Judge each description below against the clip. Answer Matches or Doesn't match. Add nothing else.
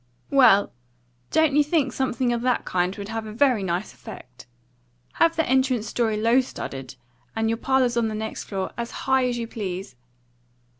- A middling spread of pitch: Matches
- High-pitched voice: Matches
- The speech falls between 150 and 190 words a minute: Matches